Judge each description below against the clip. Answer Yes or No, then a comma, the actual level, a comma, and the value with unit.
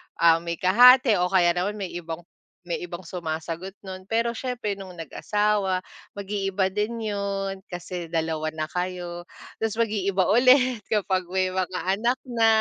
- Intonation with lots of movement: No, average, 3.0 semitones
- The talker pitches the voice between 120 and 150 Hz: No, high, 190 Hz